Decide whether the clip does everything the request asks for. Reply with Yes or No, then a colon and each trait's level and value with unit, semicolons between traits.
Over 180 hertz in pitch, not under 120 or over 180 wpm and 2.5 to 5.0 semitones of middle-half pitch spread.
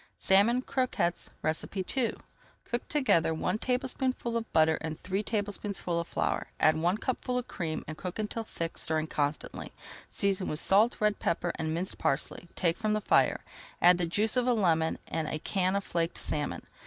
No: high, 190 Hz; average, 175 wpm; wide, 5.4 semitones